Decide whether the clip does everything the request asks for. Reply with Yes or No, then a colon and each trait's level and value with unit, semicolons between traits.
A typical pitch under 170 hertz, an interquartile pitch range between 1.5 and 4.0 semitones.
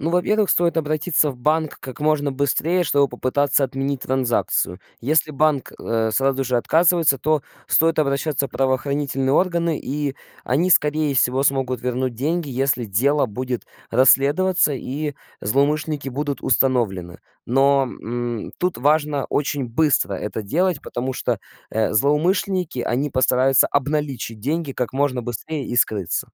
Yes: medium, 140 Hz; average, 3.3 semitones